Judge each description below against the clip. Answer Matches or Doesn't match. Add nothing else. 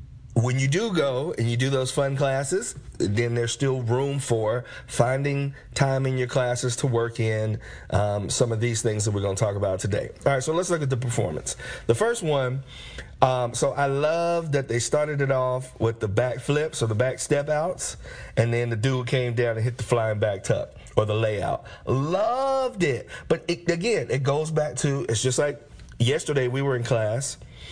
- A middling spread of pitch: Matches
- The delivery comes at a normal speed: Doesn't match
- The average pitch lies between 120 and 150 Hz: Matches